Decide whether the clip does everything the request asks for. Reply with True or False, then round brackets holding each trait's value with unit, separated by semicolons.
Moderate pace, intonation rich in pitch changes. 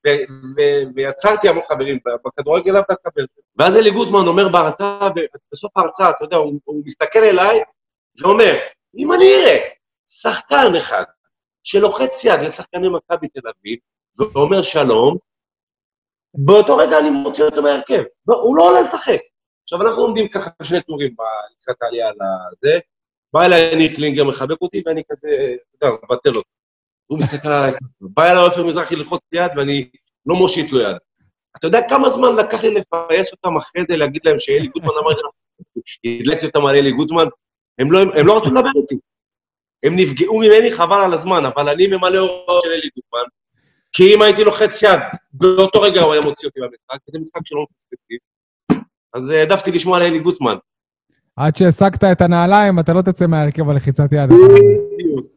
False (160 wpm; 6.2 semitones)